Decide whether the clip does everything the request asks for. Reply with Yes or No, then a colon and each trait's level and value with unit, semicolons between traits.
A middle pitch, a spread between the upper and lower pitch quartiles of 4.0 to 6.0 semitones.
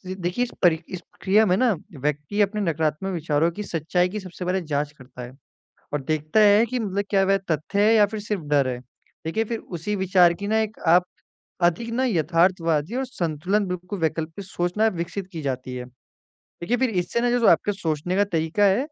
Yes: medium, 180 Hz; average, 4.7 semitones